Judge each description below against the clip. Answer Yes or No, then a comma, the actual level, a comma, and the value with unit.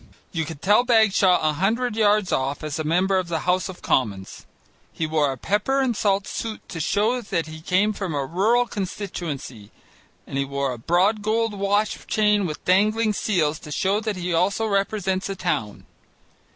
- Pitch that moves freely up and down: No, average, 5.0 semitones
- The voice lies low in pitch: No, high, 190 Hz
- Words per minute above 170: Yes, average, 185 wpm